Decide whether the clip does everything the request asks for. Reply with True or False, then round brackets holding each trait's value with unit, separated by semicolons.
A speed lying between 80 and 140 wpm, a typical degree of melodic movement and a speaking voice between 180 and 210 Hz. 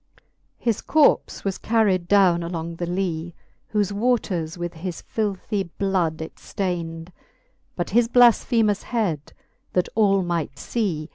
True (135 wpm; 3.9 semitones; 185 Hz)